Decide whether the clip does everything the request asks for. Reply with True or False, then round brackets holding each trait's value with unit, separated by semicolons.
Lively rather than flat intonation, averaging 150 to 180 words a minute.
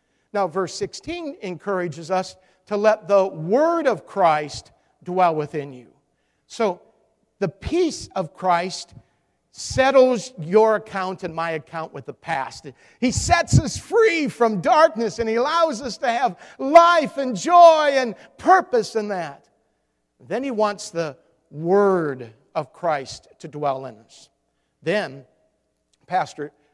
False (8.0 semitones; 135 wpm)